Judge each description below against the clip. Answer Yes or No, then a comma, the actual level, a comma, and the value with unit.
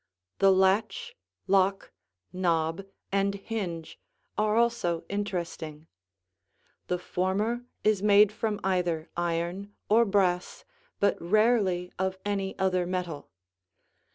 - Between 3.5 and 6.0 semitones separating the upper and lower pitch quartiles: No, average, 2.7 semitones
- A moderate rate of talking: No, slow, 100 wpm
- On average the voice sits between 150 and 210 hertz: Yes, high, 190 Hz